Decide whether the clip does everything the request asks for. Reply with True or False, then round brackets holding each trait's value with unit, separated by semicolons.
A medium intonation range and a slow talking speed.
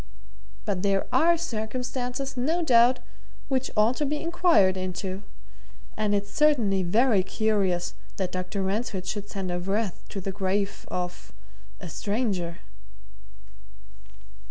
True (4.9 semitones; 125 wpm)